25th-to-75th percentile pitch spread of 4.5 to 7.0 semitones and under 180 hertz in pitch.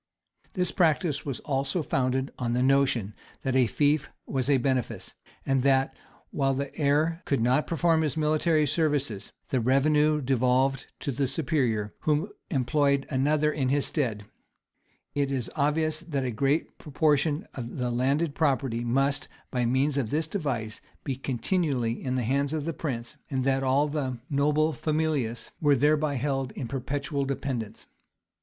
No: average, 2.7 semitones; medium, 140 Hz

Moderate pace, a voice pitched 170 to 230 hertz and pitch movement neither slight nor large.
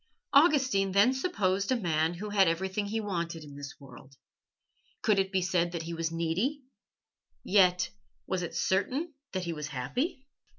Yes: average, 165 wpm; high, 190 Hz; average, 4.2 semitones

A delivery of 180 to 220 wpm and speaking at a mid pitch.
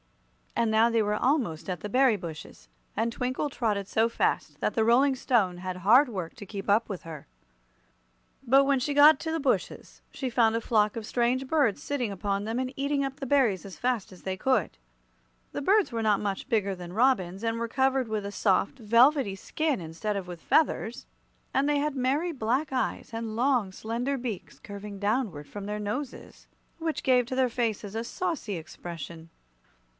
No: average, 190 wpm; high, 230 Hz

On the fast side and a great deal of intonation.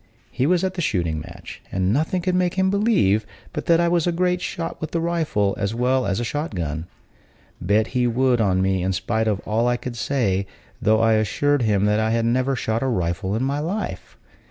Yes: fast, 225 wpm; wide, 8.0 semitones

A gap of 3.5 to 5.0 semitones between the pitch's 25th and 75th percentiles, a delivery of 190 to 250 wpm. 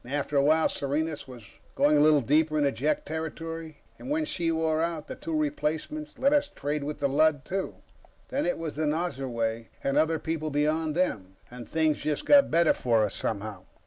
No: average, 2.7 semitones; average, 195 wpm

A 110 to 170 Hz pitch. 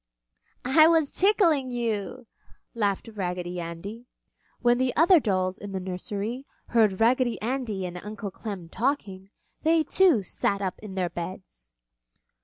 No: high, 210 Hz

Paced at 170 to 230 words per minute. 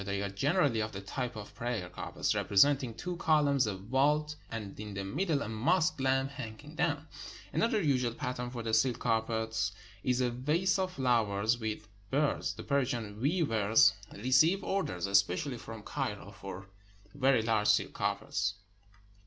No: average, 160 wpm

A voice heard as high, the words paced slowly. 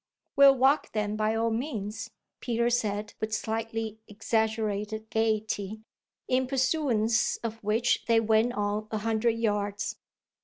Yes: high, 220 Hz; slow, 125 wpm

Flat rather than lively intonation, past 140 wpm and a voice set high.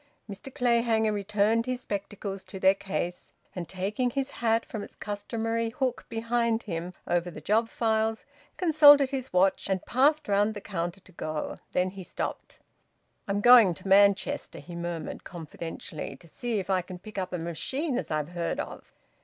No: average, 4.1 semitones; average, 170 wpm; high, 205 Hz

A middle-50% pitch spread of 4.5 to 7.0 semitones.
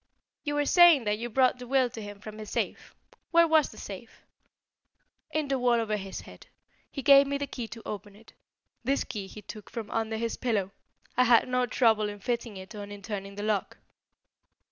No: average, 3.9 semitones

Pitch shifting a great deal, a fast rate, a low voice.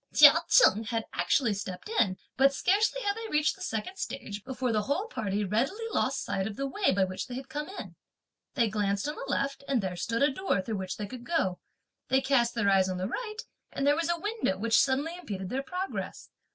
No: wide, 8.1 semitones; fast, 225 wpm; very high, 260 Hz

